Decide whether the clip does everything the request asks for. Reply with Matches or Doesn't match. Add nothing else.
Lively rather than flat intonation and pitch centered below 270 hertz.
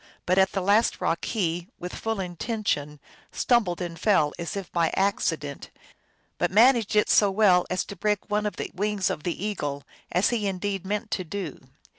Doesn't match